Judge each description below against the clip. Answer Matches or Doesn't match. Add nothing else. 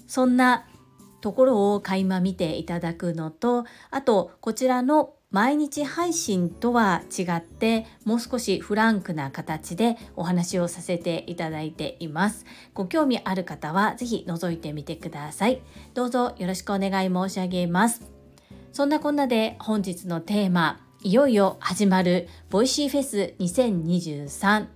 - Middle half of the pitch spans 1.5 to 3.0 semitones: Doesn't match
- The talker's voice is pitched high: Matches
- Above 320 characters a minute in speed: Doesn't match